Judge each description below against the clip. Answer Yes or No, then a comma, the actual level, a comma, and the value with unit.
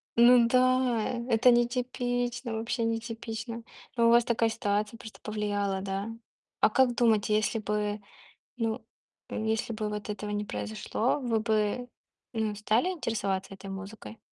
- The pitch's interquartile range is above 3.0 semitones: No, narrow, 2.4 semitones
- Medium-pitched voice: No, high, 225 Hz